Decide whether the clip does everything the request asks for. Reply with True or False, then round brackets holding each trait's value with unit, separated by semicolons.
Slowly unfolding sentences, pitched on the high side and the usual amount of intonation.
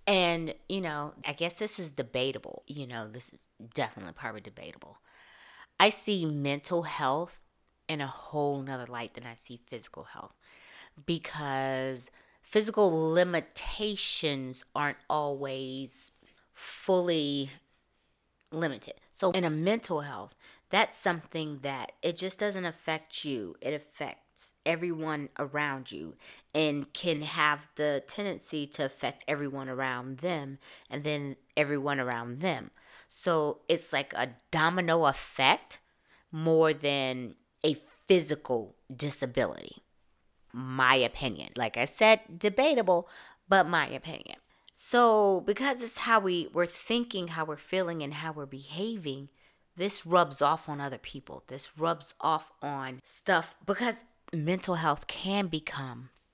False (125 wpm; 155 Hz; 4.6 semitones)